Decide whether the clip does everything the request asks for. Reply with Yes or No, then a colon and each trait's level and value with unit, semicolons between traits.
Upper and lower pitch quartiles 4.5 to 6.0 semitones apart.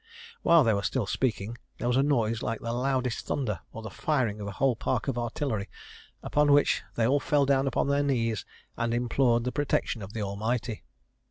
No: average, 3.5 semitones